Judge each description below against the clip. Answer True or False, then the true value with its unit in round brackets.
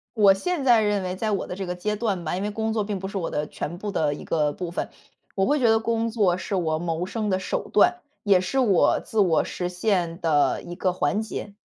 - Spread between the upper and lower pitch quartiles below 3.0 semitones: False (3.5 semitones)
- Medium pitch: False (195 Hz)